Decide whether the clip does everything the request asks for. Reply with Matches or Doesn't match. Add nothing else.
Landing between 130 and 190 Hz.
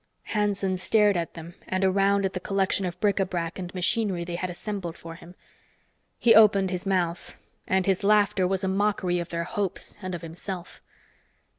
Matches